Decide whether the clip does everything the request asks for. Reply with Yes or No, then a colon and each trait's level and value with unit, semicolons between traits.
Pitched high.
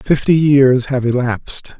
No: low, 130 Hz